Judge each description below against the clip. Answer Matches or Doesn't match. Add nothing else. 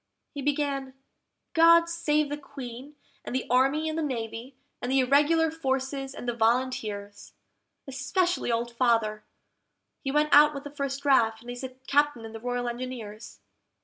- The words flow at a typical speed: Matches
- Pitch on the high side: Matches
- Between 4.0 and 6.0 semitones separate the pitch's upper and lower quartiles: Doesn't match